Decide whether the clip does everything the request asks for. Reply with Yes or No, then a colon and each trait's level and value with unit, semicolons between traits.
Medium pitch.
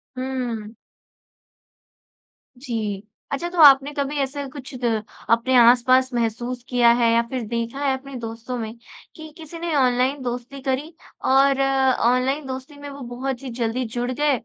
No: very high, 260 Hz